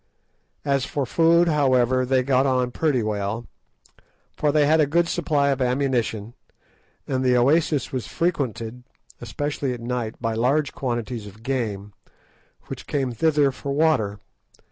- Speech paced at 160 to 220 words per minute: No, average, 145 wpm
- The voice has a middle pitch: No, low, 130 Hz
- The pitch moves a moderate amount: Yes, average, 3.5 semitones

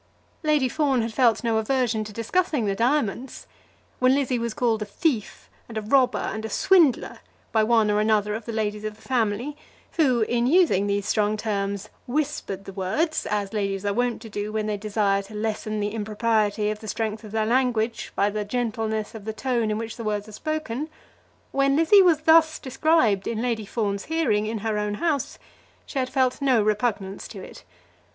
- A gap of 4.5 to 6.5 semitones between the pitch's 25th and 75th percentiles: No, average, 3.5 semitones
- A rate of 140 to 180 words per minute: No, average, 195 wpm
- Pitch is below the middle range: No, high, 220 Hz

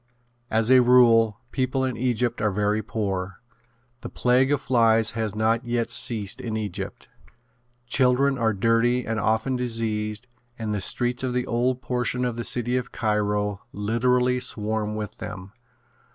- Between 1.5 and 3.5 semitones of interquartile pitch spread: Yes, average, 2.7 semitones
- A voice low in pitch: Yes, low, 115 Hz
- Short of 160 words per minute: Yes, average, 150 wpm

